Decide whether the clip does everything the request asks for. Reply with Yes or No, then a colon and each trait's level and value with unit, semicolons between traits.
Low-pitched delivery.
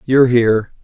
Yes: low, 120 Hz